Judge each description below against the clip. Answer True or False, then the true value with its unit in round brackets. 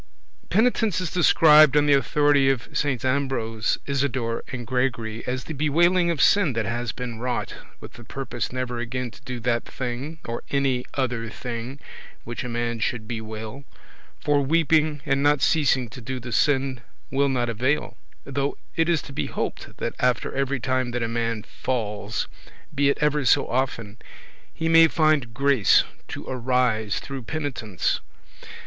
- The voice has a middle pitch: False (130 Hz)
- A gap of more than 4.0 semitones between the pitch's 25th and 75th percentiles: False (3.3 semitones)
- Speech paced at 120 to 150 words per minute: False (165 wpm)